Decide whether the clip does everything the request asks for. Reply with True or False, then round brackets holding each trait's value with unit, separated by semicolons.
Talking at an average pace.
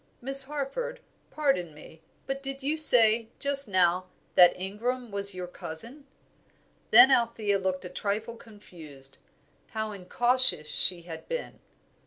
False (130 wpm)